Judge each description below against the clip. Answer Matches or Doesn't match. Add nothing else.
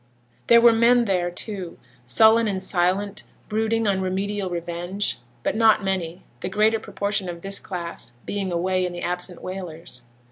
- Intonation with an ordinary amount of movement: Matches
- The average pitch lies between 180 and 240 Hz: Matches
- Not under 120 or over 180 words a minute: Matches